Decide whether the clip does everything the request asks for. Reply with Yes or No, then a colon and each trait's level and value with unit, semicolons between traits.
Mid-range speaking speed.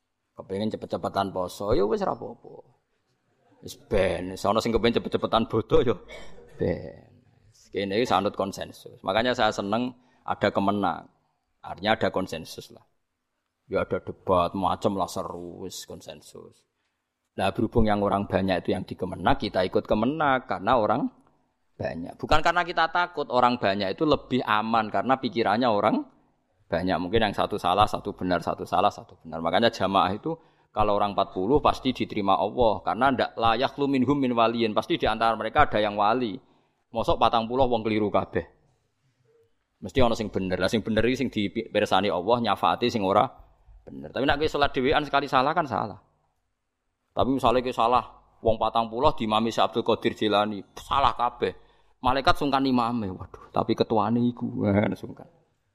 No: fast, 160 wpm